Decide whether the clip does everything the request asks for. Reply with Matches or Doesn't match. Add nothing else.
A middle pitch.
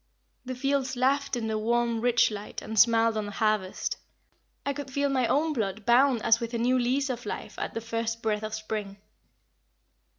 Doesn't match